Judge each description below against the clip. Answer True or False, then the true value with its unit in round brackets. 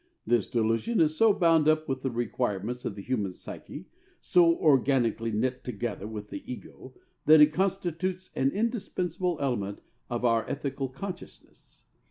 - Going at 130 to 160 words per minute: True (150 wpm)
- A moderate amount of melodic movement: False (6.4 semitones)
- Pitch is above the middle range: False (135 Hz)